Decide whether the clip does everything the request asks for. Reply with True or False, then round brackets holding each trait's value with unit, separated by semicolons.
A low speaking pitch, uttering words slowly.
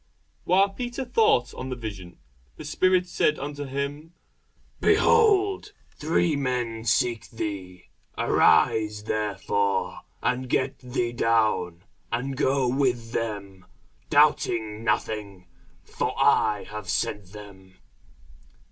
True (115 Hz; 105 wpm)